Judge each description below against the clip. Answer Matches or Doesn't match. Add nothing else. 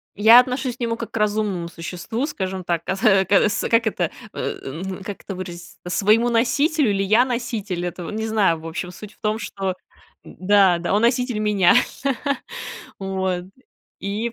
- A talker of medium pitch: Doesn't match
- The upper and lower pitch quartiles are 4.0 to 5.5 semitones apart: Doesn't match